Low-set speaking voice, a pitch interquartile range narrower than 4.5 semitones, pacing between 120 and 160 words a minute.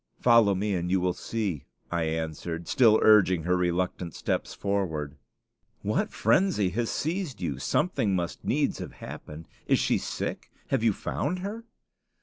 No: very low, 95 Hz; average, 5.2 semitones; average, 150 wpm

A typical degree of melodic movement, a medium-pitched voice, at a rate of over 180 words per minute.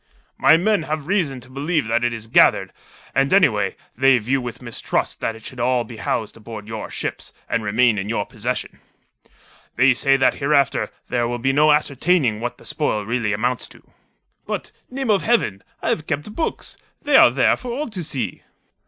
No: average, 4.9 semitones; low, 125 Hz; average, 190 wpm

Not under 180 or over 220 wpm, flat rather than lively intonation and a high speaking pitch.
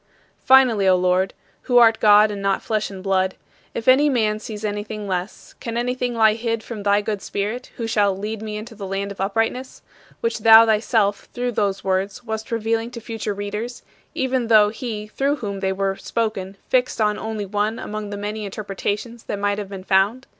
Yes: average, 195 wpm; narrow, 2.3 semitones; high, 215 Hz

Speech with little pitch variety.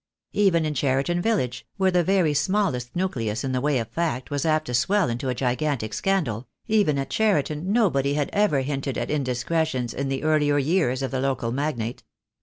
No: average, 4.9 semitones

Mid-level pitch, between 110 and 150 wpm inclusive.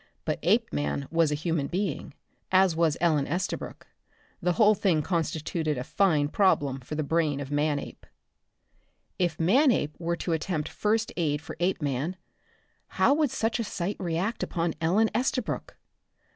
Yes: medium, 165 Hz; average, 145 wpm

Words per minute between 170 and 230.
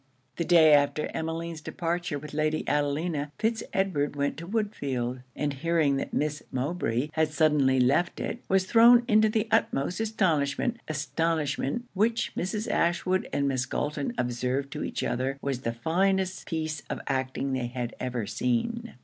No: average, 155 wpm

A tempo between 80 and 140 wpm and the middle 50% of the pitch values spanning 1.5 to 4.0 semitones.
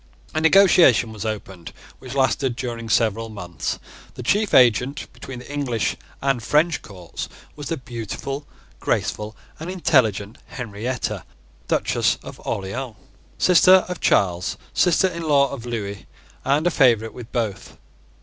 No: slow, 135 wpm; average, 5.0 semitones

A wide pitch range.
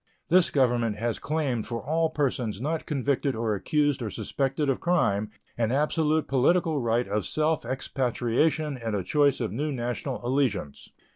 No: average, 4.5 semitones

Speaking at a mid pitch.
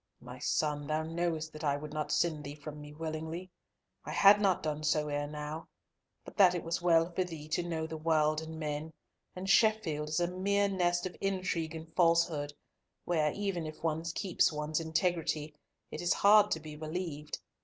Yes: medium, 160 Hz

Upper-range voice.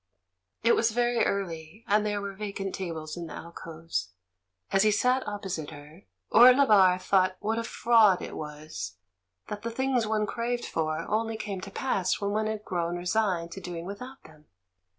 Yes: high, 200 Hz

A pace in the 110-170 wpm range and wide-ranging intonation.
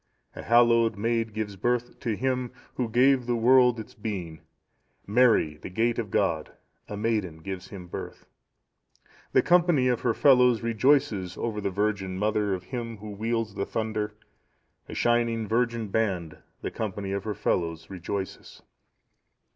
No: average, 150 wpm; average, 3.2 semitones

